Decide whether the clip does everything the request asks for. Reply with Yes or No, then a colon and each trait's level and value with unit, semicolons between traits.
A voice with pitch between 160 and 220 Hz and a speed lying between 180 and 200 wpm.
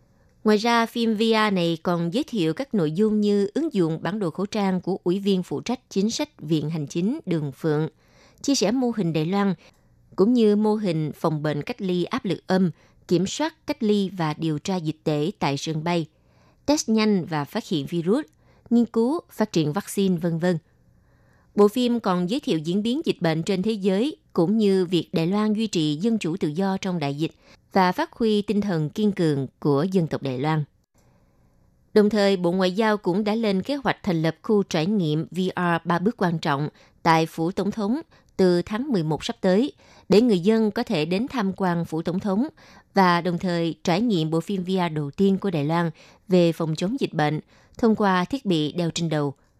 No: medium, 185 Hz; average, 210 wpm